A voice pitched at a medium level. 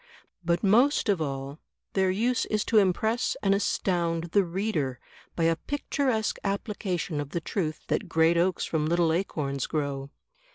Yes: medium, 175 Hz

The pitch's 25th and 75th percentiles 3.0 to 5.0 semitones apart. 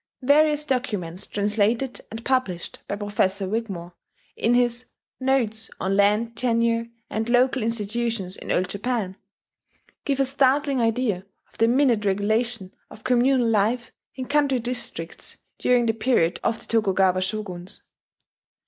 Yes: average, 3.7 semitones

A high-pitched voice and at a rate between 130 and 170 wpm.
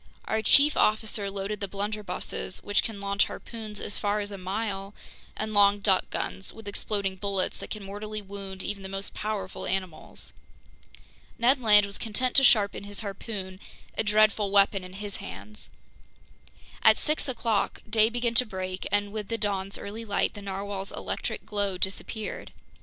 Yes: high, 205 Hz; average, 165 wpm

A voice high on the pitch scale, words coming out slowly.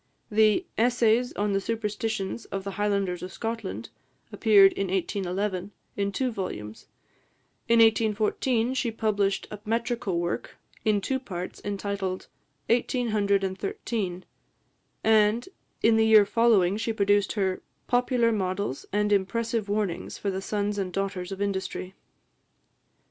Yes: high, 205 Hz; slow, 130 wpm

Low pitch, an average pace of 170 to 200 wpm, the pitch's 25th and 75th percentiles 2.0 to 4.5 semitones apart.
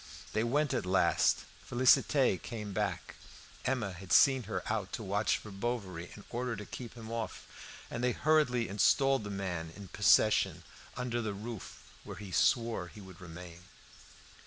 No: low, 110 Hz; average, 160 wpm; average, 3.9 semitones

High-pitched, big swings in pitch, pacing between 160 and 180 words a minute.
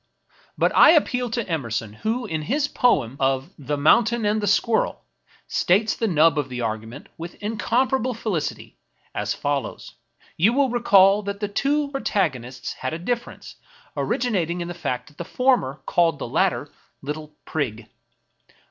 No: medium, 175 Hz; wide, 8.4 semitones; average, 165 wpm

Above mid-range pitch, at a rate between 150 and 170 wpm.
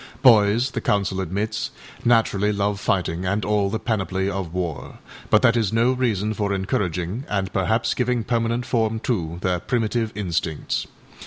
No: low, 105 Hz; average, 160 wpm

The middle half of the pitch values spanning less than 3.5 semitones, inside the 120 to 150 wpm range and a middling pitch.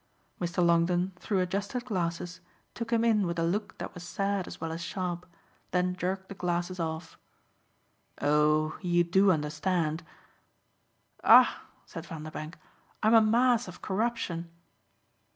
Yes: average, 2.8 semitones; slow, 135 wpm; medium, 180 Hz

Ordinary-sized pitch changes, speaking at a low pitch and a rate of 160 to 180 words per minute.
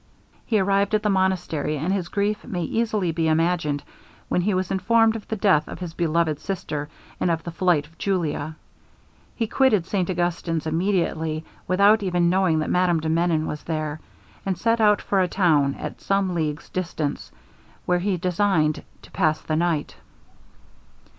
No: average, 3.6 semitones; medium, 175 Hz; average, 170 wpm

